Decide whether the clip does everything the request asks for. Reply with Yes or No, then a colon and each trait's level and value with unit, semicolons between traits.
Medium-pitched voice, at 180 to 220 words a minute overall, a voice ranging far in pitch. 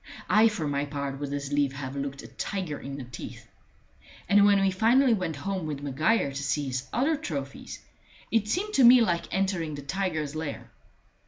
Yes: medium, 155 Hz; average, 190 wpm; wide, 6.3 semitones